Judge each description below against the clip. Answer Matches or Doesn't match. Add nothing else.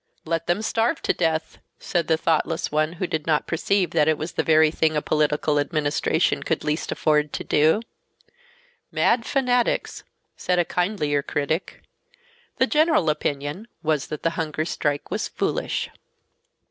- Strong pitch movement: Doesn't match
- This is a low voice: Doesn't match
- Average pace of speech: Matches